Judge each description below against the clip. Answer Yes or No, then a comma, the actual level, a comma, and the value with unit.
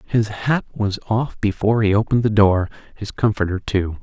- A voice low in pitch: Yes, low, 105 Hz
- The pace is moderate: Yes, average, 180 wpm